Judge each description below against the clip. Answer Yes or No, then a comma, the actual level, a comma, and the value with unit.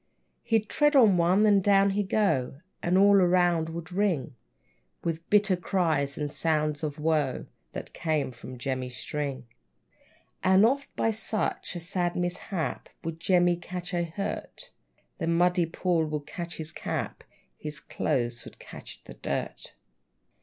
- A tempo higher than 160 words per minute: No, average, 145 wpm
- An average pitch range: Yes, average, 4.2 semitones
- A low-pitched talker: No, medium, 175 Hz